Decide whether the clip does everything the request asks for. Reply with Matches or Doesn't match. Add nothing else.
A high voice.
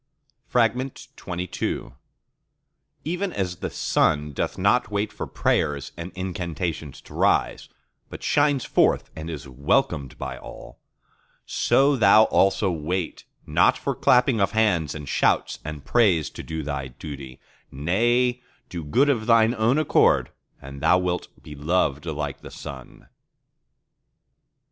Doesn't match